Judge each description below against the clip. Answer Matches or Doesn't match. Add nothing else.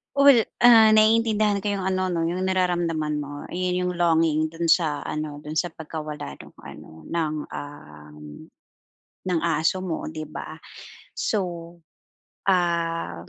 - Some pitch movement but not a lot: Matches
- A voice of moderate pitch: Matches